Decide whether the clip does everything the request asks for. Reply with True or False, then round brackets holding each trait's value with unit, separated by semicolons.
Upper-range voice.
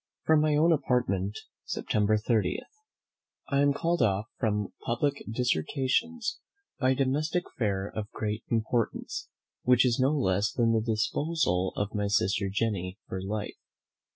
False (115 Hz)